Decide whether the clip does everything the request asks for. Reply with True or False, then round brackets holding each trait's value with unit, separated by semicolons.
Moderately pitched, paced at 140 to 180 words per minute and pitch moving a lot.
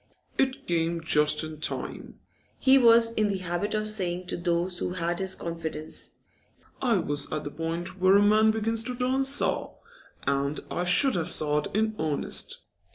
False (180 Hz; 170 wpm; 5.0 semitones)